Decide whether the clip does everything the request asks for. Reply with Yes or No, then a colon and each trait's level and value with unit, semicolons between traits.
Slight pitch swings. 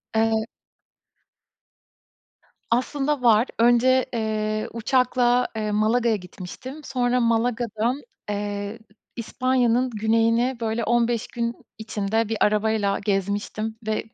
Yes: narrow, 2.2 semitones